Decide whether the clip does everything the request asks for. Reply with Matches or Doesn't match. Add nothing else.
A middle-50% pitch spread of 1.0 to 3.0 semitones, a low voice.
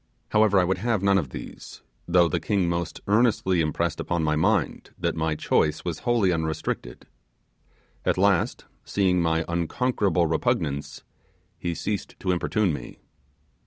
Doesn't match